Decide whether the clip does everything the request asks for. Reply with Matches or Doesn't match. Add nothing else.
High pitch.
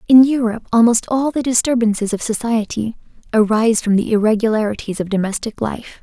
Matches